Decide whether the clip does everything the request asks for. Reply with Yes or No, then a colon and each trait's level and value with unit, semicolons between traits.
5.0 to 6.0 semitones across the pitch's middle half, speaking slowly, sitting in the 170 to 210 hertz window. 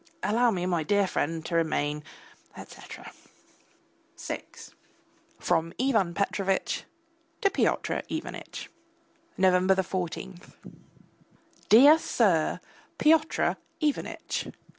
Yes: wide, 5.6 semitones; slow, 85 wpm; high, 190 Hz